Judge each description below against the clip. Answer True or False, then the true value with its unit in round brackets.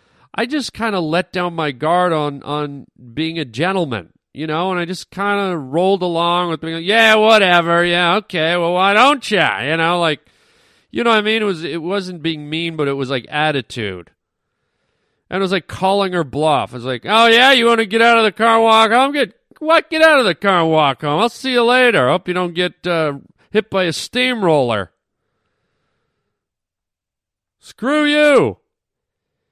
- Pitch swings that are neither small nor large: False (6.2 semitones)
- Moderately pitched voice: True (180 Hz)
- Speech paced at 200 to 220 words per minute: True (205 wpm)